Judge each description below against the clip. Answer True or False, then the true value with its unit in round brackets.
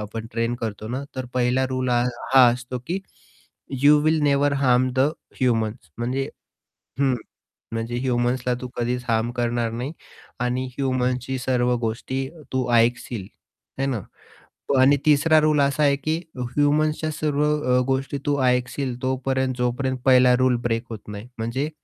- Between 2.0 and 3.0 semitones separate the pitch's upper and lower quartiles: True (2.4 semitones)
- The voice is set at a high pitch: False (130 Hz)